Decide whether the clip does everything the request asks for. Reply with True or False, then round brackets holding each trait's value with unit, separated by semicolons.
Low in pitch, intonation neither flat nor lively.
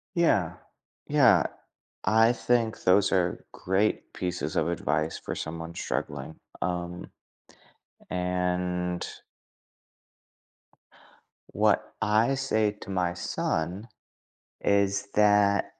True (90 Hz; 3.2 semitones)